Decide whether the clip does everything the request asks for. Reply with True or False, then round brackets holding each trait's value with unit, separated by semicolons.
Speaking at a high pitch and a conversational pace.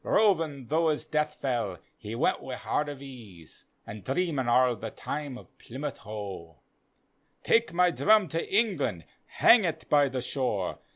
False (135 Hz; 170 wpm)